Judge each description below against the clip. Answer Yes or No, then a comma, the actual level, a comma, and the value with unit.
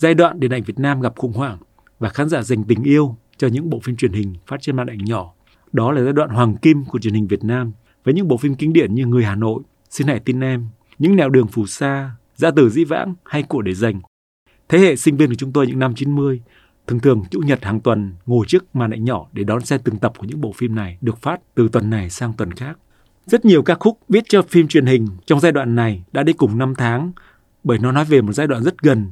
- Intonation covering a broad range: No, average, 4.8 semitones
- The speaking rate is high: Yes, fast, 270 wpm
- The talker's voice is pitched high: No, low, 125 Hz